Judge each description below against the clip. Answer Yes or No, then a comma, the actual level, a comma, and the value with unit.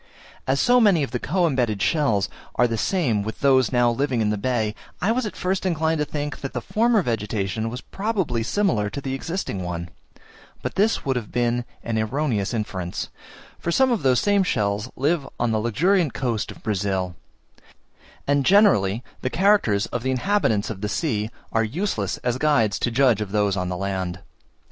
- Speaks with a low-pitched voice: Yes, low, 125 Hz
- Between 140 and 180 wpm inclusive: No, average, 190 wpm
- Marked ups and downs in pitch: Yes, wide, 7.2 semitones